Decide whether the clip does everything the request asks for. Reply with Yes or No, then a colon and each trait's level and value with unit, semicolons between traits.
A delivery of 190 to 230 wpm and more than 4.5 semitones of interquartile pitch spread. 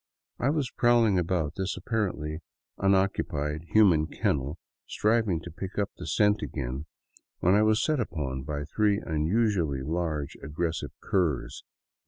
No: slow, 135 wpm; wide, 5.6 semitones